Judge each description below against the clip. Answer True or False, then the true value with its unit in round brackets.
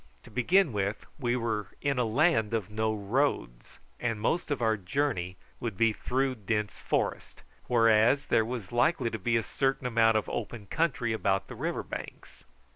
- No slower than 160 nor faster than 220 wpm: True (175 wpm)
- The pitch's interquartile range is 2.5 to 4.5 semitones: True (3.3 semitones)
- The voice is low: True (115 Hz)